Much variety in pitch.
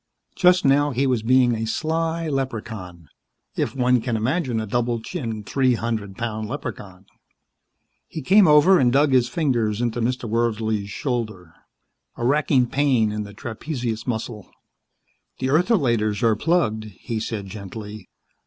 No: average, 4.0 semitones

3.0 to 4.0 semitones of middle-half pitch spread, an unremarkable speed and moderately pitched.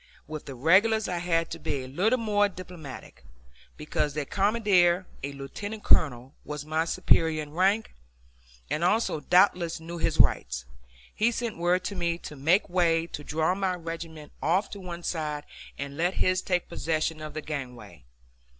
Yes: average, 3.4 semitones; average, 170 wpm; medium, 170 Hz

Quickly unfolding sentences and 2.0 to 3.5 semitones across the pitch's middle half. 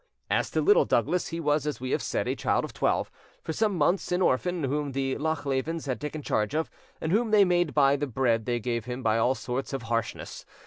No: fast, 230 wpm; average, 4.6 semitones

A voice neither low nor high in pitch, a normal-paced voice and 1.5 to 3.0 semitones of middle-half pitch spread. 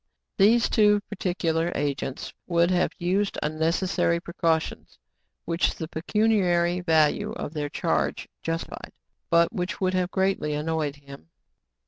No: medium, 170 Hz; slow, 120 wpm; average, 2.7 semitones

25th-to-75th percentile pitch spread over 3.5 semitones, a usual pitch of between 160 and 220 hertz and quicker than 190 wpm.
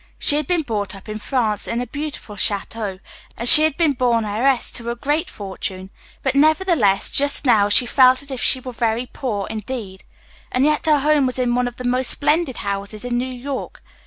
No: average, 4.6 semitones; high, 245 Hz; fast, 205 wpm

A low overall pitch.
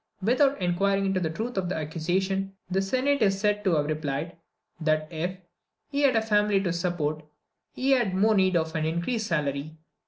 No: high, 190 Hz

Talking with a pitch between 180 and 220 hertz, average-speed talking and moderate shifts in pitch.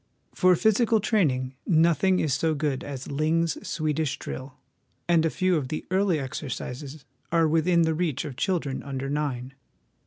No: medium, 155 Hz; average, 155 wpm; average, 3.8 semitones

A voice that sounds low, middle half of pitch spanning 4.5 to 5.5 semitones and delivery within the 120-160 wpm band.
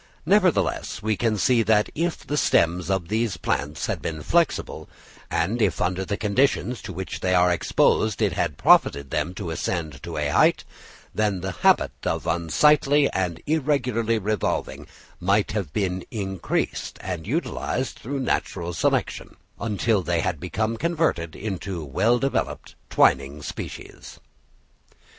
Yes: low, 100 Hz; average, 5.0 semitones; average, 145 wpm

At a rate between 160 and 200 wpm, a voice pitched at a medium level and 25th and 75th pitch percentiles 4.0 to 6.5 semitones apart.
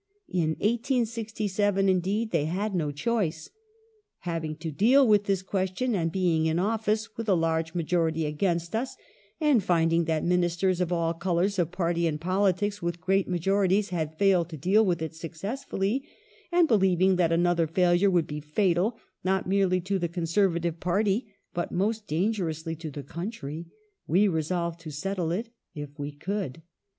No: average, 165 wpm; medium, 180 Hz; average, 3.5 semitones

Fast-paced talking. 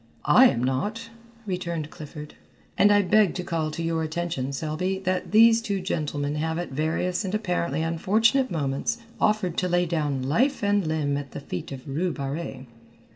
No: average, 175 wpm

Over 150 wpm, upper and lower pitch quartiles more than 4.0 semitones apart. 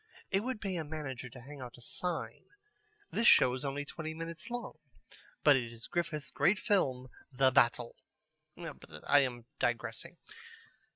Yes: average, 160 wpm; average, 5.1 semitones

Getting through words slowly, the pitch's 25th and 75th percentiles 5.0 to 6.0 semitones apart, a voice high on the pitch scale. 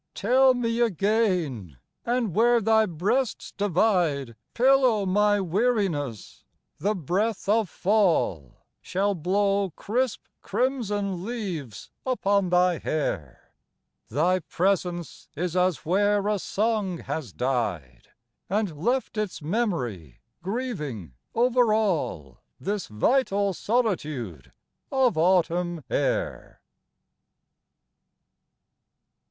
Yes: slow, 90 wpm; wide, 5.6 semitones; high, 195 Hz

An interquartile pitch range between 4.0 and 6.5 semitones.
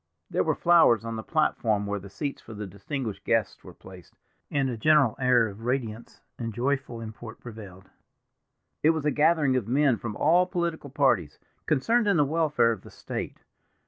Yes: wide, 5.4 semitones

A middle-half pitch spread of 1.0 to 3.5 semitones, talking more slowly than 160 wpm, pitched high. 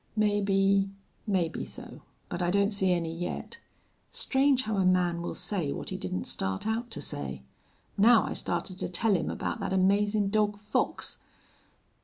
No: average, 3.1 semitones; average, 165 wpm; high, 195 Hz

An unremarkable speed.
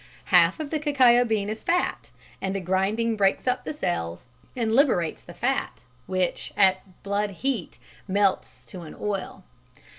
Yes: average, 155 wpm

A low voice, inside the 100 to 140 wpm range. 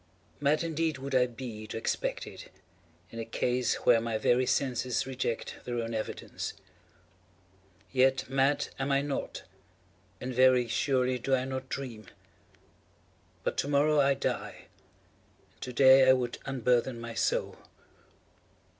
Yes: low, 130 Hz; slow, 135 wpm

